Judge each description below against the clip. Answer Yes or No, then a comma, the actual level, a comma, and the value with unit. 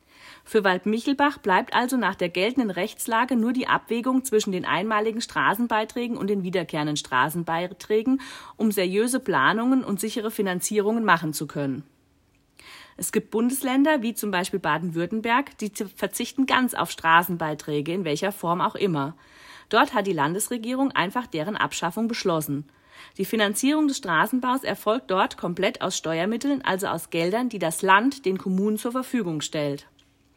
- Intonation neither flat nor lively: No, wide, 5.8 semitones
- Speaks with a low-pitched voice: No, high, 205 Hz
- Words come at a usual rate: Yes, average, 145 wpm